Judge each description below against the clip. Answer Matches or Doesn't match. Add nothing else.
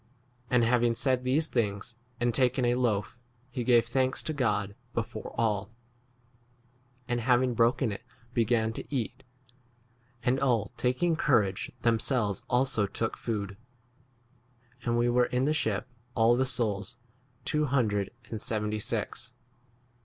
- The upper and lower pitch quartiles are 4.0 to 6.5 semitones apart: Doesn't match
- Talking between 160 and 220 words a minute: Doesn't match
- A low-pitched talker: Matches